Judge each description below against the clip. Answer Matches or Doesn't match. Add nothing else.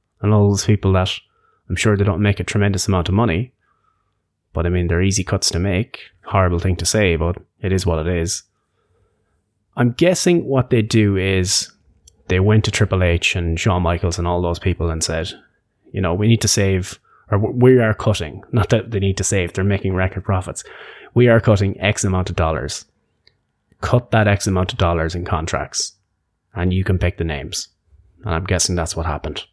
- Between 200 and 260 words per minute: Matches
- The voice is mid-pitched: Doesn't match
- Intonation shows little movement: Doesn't match